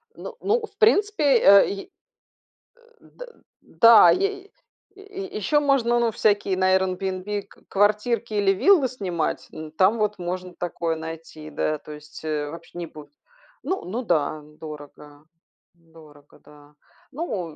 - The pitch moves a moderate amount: No, wide, 7.2 semitones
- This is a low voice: No, high, 190 Hz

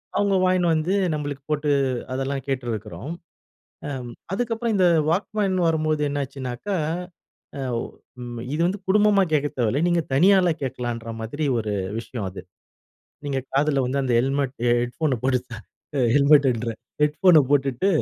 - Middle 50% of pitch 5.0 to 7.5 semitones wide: Yes, wide, 5.5 semitones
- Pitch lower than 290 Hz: Yes, medium, 140 Hz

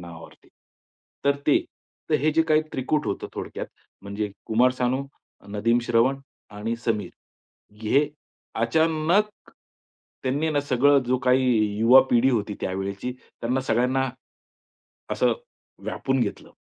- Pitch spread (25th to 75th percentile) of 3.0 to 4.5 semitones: Yes, average, 4.1 semitones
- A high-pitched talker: No, low, 125 Hz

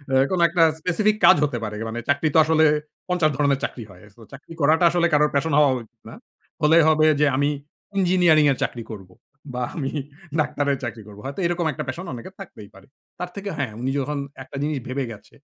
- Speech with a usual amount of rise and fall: Yes, average, 4.5 semitones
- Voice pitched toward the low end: No, medium, 150 Hz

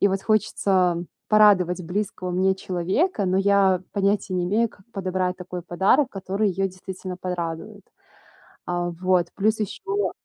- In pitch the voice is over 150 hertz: Yes, high, 190 Hz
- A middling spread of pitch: No, narrow, 2.1 semitones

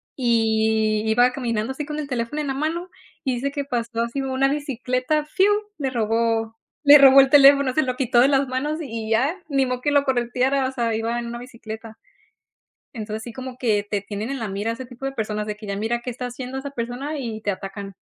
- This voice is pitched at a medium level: No, high, 245 Hz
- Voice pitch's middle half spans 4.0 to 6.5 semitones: No, average, 3.3 semitones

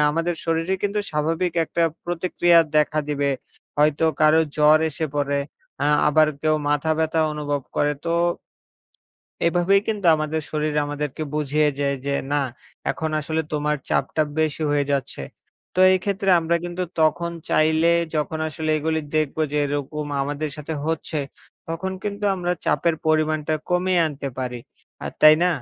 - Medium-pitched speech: Yes, medium, 155 Hz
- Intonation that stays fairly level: Yes, narrow, 2.2 semitones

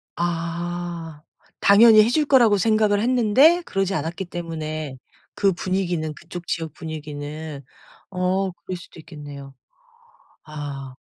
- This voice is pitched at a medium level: Yes, medium, 175 Hz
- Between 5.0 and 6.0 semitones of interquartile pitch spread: No, average, 4.3 semitones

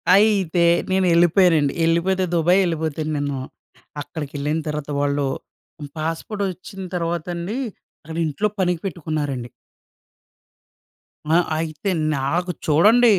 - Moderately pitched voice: Yes, medium, 165 Hz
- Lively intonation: No, average, 3.6 semitones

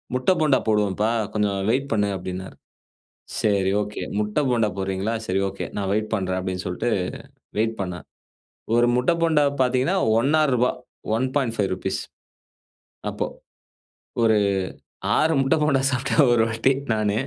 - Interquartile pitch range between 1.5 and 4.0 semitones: No, average, 4.8 semitones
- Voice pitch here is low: Yes, low, 110 Hz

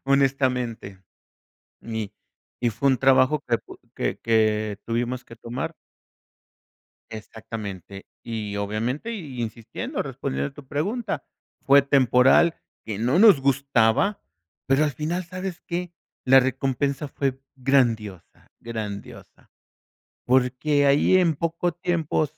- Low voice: Yes, low, 130 Hz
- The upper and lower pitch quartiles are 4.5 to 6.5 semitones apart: Yes, average, 4.9 semitones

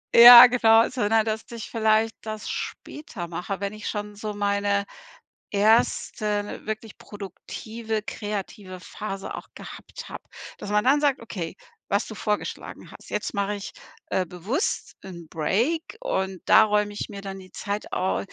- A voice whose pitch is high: Yes, high, 210 Hz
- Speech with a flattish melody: Yes, narrow, 2.0 semitones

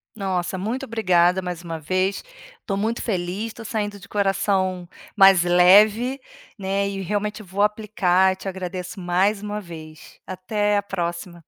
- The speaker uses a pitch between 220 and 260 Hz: No, high, 195 Hz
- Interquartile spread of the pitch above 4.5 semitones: No, narrow, 2.6 semitones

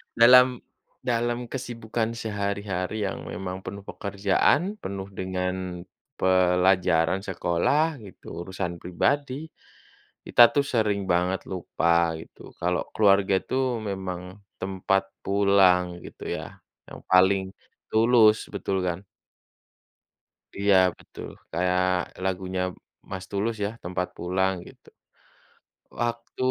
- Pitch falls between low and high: No, very low, 95 Hz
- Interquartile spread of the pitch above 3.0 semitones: Yes, average, 3.4 semitones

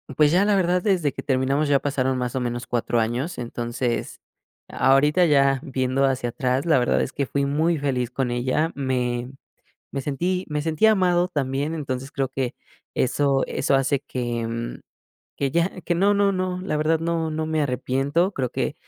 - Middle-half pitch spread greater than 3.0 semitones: Yes, average, 4.2 semitones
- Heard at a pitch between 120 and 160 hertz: Yes, medium, 140 Hz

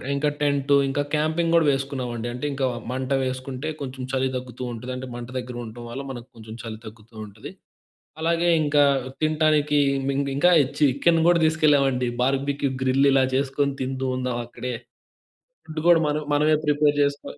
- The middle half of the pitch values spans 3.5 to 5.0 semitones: No, narrow, 2.6 semitones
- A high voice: No, low, 135 Hz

